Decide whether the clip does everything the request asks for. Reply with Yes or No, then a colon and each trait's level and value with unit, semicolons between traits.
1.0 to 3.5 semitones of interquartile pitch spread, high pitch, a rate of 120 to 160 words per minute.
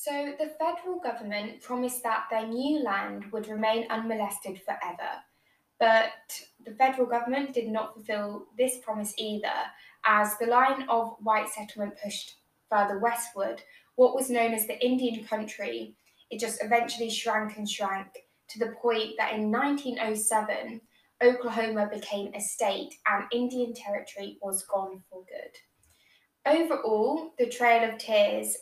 Yes: average, 2.8 semitones; high, 225 Hz; average, 140 wpm